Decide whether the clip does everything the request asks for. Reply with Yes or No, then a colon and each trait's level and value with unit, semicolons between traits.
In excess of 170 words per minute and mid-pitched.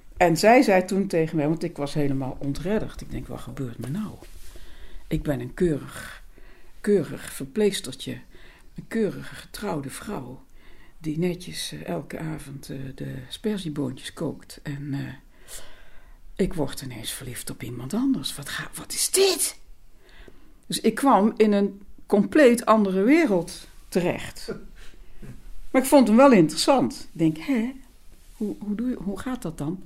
No: average, 150 wpm; medium, 175 Hz